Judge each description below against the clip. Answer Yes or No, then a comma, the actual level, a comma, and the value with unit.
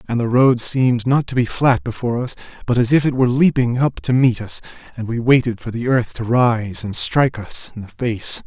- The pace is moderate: No, fast, 240 wpm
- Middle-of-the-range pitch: No, low, 120 Hz